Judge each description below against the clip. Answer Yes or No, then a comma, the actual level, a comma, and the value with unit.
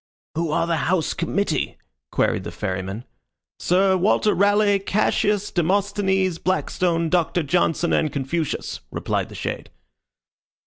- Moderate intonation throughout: Yes, average, 3.3 semitones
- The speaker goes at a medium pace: No, slow, 120 wpm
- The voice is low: No, medium, 180 Hz